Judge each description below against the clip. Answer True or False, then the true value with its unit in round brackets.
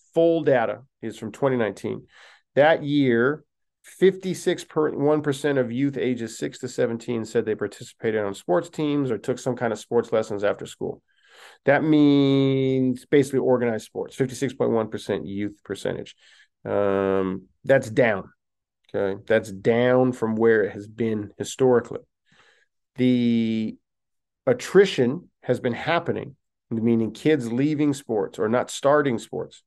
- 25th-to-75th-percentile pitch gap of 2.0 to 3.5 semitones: False (4.1 semitones)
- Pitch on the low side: True (125 Hz)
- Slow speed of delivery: True (125 wpm)